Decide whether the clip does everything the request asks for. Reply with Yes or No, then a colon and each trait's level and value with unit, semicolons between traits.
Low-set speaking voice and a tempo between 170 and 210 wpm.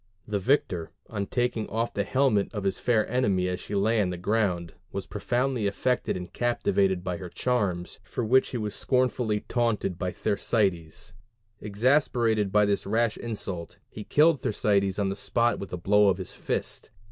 Yes: low, 105 Hz; average, 175 wpm